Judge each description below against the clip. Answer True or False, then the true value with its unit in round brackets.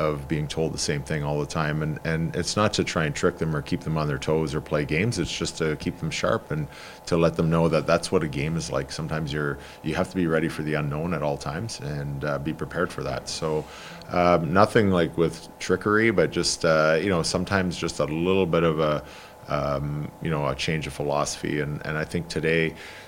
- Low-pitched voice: True (80 Hz)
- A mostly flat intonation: True (2.0 semitones)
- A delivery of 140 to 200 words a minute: False (245 wpm)